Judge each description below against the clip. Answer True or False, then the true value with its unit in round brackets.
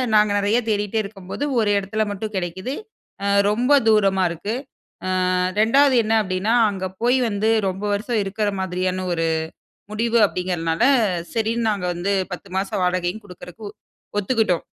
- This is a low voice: False (205 Hz)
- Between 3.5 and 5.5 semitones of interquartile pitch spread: False (3.0 semitones)